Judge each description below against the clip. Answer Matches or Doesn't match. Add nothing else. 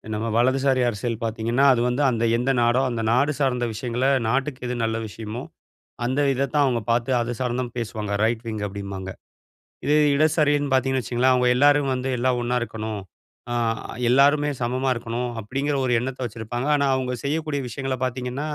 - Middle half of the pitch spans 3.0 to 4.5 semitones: Doesn't match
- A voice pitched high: Doesn't match